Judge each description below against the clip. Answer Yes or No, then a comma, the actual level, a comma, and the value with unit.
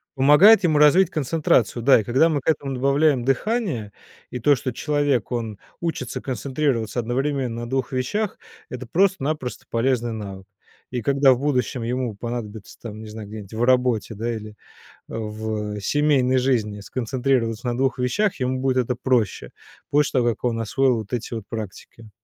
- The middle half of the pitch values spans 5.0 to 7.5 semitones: No, average, 3.5 semitones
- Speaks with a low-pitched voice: Yes, low, 125 Hz